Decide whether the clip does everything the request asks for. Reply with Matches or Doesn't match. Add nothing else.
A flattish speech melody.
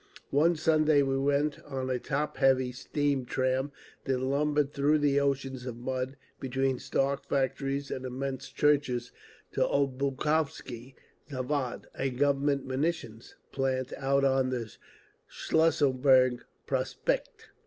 Matches